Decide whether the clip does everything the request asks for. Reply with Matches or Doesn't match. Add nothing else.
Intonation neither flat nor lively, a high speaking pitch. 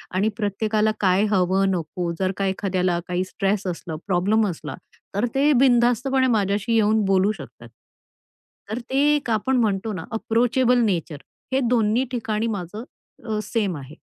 Matches